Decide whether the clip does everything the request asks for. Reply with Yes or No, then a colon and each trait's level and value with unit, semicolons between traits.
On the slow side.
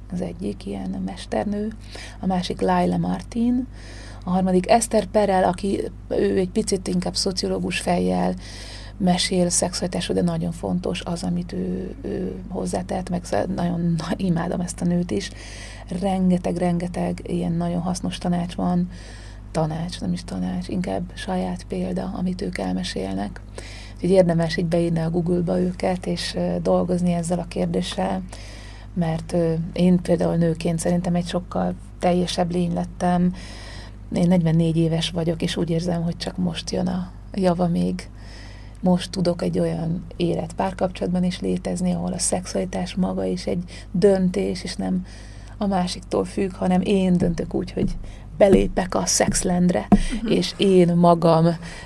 No: average, 140 wpm